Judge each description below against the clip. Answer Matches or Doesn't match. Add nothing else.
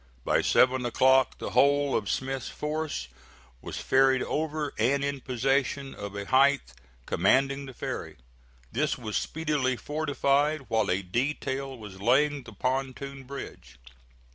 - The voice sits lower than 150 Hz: Matches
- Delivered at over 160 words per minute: Doesn't match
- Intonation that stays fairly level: Matches